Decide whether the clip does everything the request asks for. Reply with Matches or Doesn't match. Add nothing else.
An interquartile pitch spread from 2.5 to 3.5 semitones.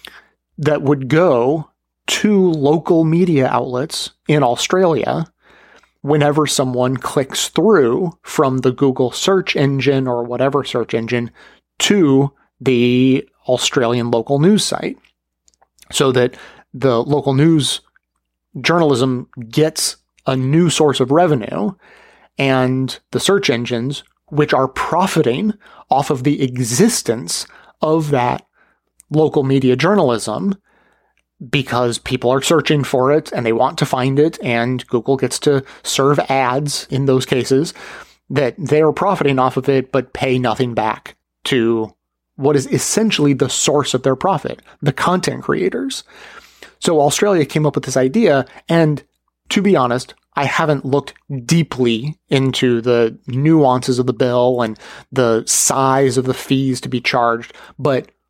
Matches